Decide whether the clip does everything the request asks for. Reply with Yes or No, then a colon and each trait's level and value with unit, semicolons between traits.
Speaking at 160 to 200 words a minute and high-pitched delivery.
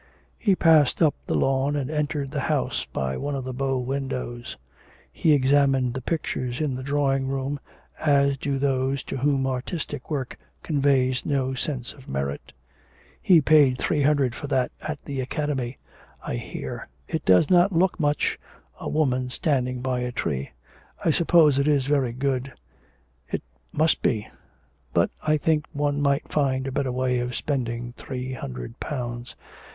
No: average, 165 wpm; low, 135 Hz